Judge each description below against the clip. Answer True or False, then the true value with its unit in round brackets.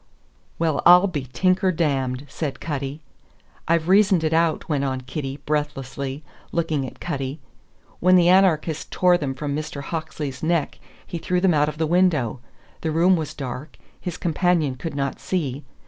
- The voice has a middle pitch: True (155 Hz)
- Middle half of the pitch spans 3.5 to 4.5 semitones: True (3.9 semitones)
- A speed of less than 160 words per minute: False (165 wpm)